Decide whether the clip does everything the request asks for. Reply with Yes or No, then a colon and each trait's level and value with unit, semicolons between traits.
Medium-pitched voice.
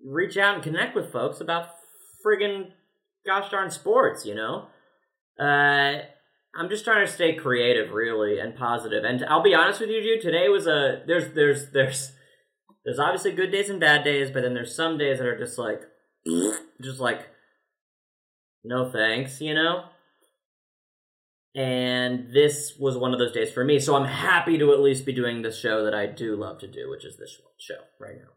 Yes: medium, 145 Hz